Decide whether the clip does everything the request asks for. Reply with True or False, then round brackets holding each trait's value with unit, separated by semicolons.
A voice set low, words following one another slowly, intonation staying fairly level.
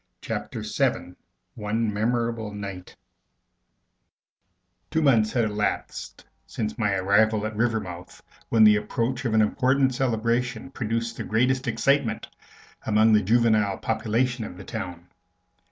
True (110 Hz; 120 wpm; 2.3 semitones)